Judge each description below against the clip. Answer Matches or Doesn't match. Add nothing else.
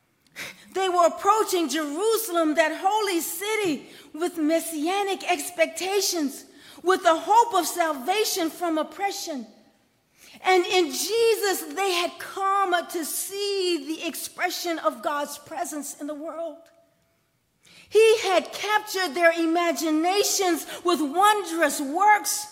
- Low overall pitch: Doesn't match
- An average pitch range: Matches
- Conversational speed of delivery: Doesn't match